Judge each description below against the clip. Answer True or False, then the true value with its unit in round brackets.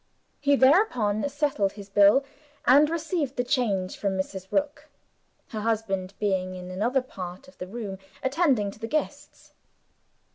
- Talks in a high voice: True (225 Hz)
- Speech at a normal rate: True (145 wpm)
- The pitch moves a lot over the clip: True (6.4 semitones)